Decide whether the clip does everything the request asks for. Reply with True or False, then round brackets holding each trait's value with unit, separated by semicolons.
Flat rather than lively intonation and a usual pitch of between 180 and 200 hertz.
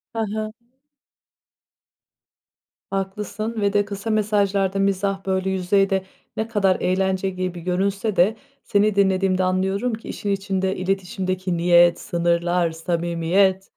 True (1.6 semitones; 190 Hz)